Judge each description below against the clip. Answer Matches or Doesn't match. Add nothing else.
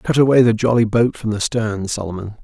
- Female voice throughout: Doesn't match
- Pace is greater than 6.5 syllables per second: Doesn't match